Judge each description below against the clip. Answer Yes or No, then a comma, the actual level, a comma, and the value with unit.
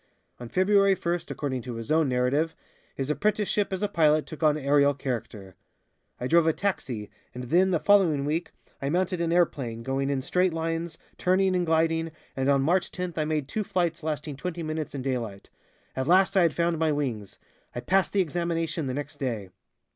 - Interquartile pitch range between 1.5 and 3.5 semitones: No, average, 4.5 semitones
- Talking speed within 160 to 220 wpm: Yes, average, 190 wpm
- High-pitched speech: No, medium, 155 Hz